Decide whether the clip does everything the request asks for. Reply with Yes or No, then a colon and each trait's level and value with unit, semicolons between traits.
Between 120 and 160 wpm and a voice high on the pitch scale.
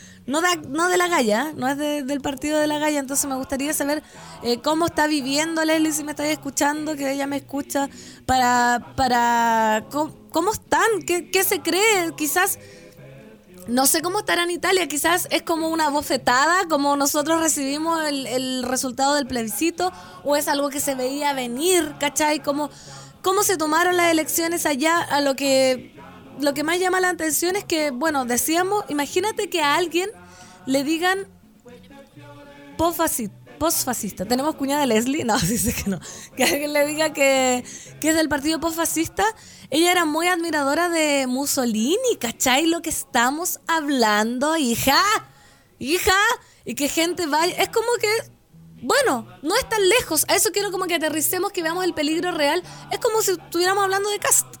No: average, 170 wpm; very high, 305 Hz